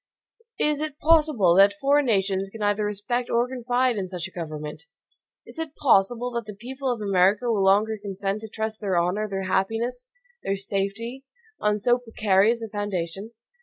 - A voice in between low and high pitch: No, high, 210 Hz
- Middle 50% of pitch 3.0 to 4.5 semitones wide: Yes, average, 3.9 semitones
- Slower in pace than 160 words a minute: No, average, 170 wpm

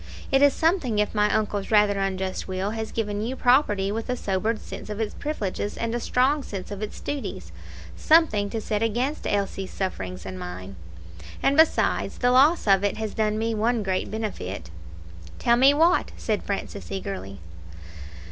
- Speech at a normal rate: Yes, average, 175 wpm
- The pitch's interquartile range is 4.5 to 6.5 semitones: No, average, 4.0 semitones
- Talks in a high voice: Yes, high, 215 Hz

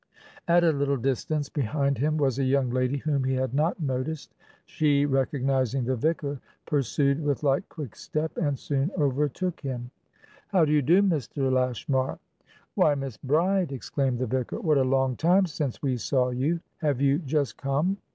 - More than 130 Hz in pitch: Yes, medium, 140 Hz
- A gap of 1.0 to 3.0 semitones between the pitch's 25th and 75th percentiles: Yes, average, 2.7 semitones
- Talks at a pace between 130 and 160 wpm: No, average, 170 wpm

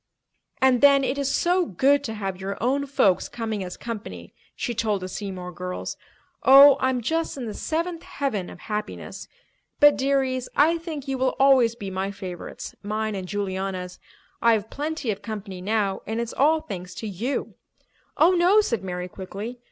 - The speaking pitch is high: Yes, high, 225 Hz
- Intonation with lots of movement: Yes, wide, 6.1 semitones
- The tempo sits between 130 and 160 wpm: No, average, 170 wpm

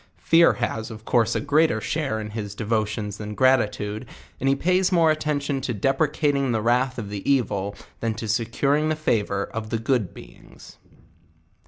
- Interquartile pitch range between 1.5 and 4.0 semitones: No, average, 4.8 semitones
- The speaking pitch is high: No, low, 120 Hz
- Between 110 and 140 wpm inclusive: No, average, 180 wpm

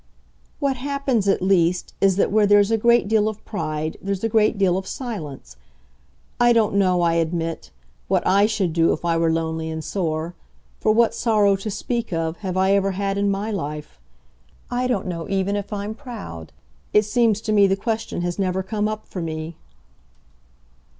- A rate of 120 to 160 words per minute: No, average, 190 wpm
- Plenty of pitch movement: No, average, 4.1 semitones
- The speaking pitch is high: Yes, high, 195 Hz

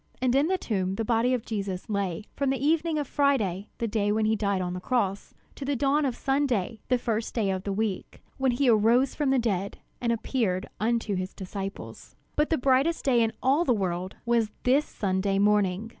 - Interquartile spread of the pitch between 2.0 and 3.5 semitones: No, average, 5.0 semitones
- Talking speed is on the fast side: Yes, fast, 210 wpm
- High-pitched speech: Yes, high, 225 Hz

